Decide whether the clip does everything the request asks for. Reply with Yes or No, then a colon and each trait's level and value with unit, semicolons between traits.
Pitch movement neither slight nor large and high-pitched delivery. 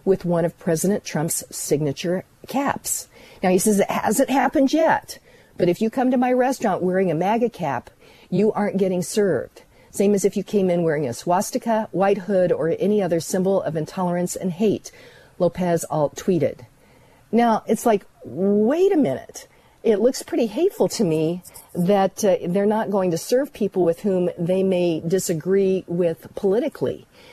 Yes: average, 4.0 semitones; high, 195 Hz